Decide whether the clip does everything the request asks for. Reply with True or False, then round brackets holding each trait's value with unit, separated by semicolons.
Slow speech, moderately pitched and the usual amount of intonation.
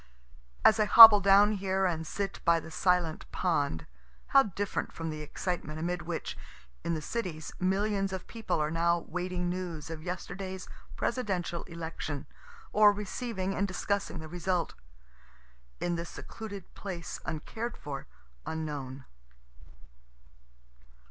True (130 wpm; 180 Hz; 3.5 semitones)